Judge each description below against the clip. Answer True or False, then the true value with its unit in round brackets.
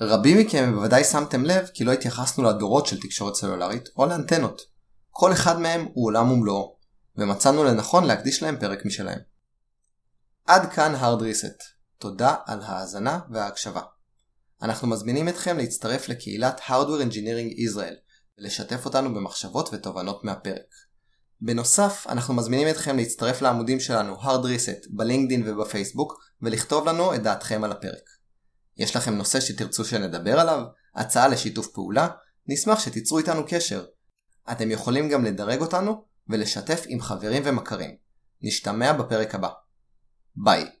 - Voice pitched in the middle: False (120 Hz)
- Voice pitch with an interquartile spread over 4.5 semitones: True (4.9 semitones)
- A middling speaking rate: True (130 wpm)